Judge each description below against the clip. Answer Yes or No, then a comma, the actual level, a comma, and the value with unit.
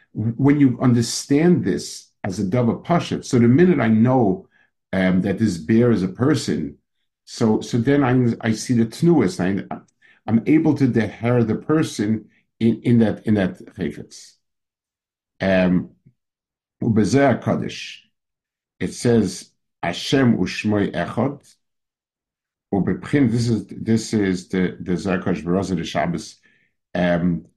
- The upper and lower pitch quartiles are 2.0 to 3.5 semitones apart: No, average, 4.8 semitones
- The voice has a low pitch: Yes, low, 115 Hz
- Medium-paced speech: No, slow, 120 wpm